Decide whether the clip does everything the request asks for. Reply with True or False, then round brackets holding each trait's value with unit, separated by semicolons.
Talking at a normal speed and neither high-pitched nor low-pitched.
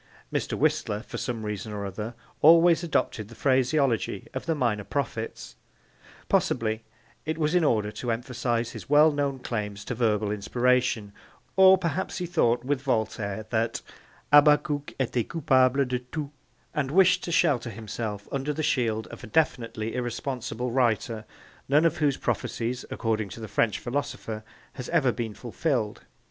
False (155 wpm; 125 Hz)